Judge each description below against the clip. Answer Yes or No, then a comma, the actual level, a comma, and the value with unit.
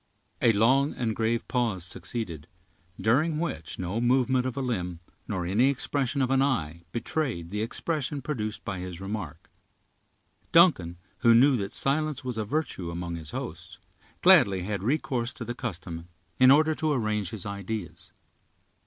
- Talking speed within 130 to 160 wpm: Yes, average, 155 wpm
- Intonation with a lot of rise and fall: Yes, wide, 6.3 semitones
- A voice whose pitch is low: Yes, low, 115 Hz